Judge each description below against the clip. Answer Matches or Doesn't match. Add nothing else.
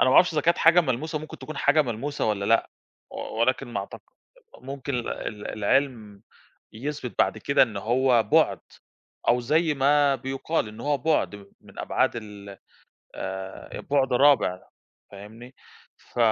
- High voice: Doesn't match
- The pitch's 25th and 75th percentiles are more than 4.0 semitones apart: Matches